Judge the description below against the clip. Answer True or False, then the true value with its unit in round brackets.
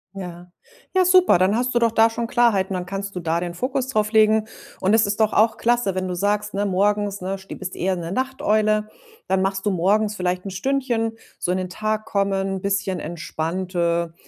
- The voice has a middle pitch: False (200 Hz)